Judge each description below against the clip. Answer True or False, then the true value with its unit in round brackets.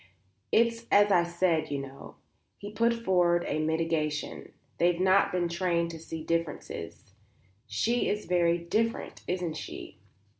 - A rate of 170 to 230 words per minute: False (140 wpm)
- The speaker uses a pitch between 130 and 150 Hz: False (175 Hz)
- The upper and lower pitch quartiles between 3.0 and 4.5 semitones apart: True (3.3 semitones)